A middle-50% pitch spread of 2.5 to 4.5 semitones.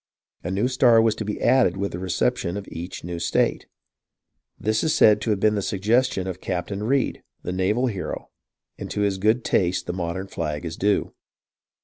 Yes: average, 3.3 semitones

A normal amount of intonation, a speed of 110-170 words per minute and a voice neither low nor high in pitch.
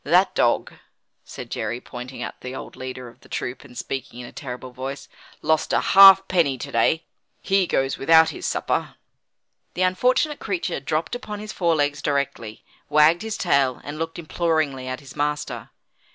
Yes: average, 4.8 semitones; average, 165 wpm; medium, 150 Hz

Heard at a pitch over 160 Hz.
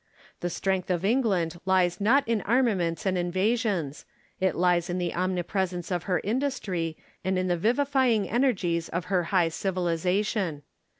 Yes: medium, 185 Hz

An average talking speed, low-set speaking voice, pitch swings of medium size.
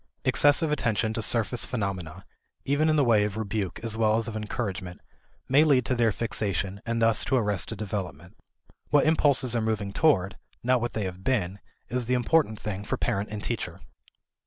Yes: average, 180 wpm; low, 110 Hz; average, 3.9 semitones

